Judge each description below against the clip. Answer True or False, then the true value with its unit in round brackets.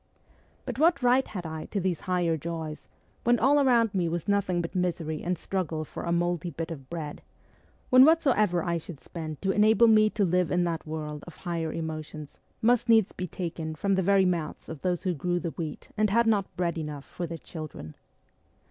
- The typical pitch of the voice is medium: True (175 Hz)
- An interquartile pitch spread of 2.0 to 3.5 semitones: False (4.2 semitones)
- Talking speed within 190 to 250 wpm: True (200 wpm)